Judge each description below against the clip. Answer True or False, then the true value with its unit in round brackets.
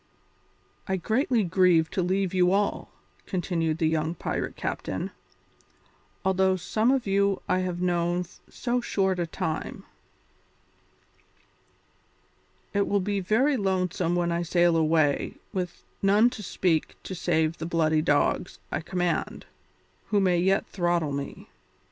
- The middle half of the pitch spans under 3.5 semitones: True (2.8 semitones)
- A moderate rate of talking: False (130 wpm)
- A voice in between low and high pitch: True (180 Hz)